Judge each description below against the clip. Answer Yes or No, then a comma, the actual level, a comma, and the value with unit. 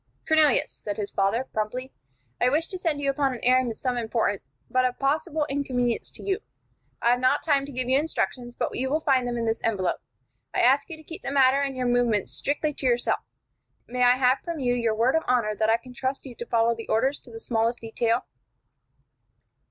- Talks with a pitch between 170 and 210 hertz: No, very high, 250 Hz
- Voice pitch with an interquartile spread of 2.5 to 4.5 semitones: Yes, average, 3.0 semitones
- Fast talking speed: Yes, fast, 220 wpm